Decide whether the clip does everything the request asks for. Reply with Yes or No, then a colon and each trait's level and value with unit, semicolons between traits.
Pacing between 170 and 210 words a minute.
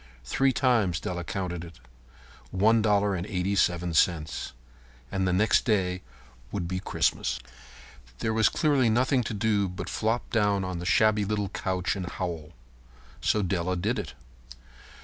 No: average, 150 wpm